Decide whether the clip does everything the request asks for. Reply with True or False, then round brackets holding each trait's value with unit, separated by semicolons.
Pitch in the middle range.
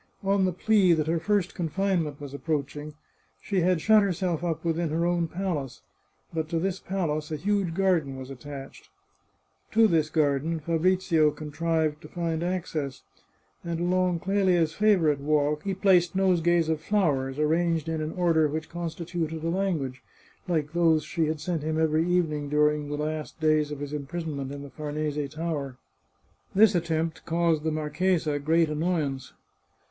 True (160 Hz)